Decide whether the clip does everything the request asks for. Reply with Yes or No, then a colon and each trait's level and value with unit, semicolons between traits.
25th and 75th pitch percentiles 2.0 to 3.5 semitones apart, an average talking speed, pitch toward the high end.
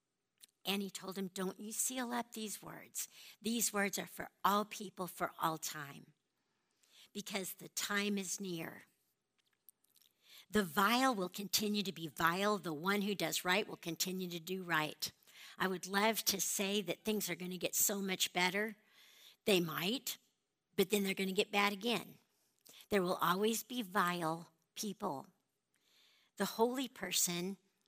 Yes: narrow, 2.6 semitones; average, 160 wpm; high, 195 Hz